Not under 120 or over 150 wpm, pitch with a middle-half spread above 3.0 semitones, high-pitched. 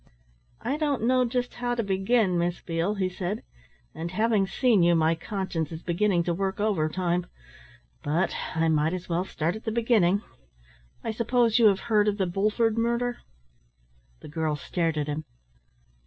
No: average, 170 wpm; average, 5.0 semitones; high, 195 Hz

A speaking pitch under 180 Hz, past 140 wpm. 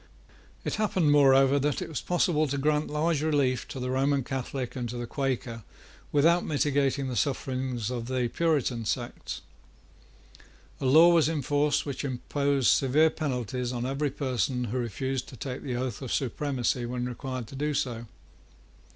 Yes: low, 135 Hz; average, 165 wpm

